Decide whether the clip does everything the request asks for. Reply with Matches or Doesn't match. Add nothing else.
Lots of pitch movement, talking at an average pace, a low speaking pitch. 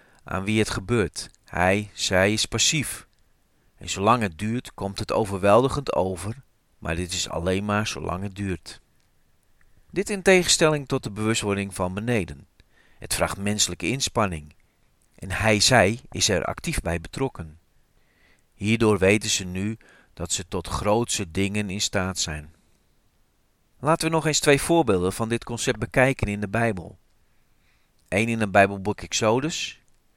Doesn't match